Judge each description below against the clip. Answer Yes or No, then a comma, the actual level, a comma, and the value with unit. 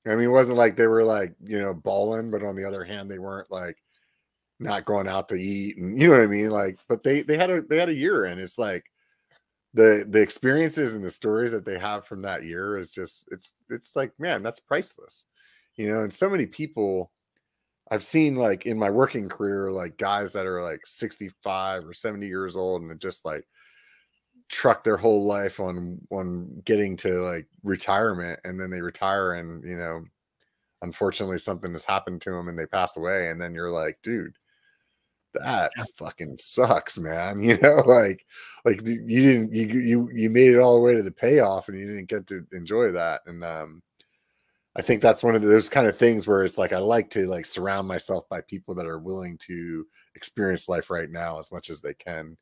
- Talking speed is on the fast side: Yes, fast, 210 wpm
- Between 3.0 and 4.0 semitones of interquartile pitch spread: Yes, average, 3.7 semitones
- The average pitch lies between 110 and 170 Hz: No, low, 100 Hz